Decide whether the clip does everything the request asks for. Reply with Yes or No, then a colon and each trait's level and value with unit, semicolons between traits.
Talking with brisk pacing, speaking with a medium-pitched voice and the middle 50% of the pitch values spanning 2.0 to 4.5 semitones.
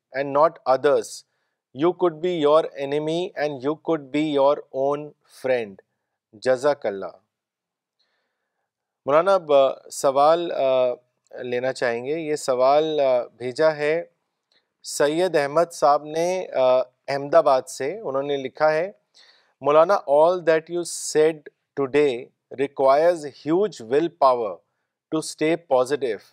No: slow, 110 wpm; medium, 150 Hz; average, 3.5 semitones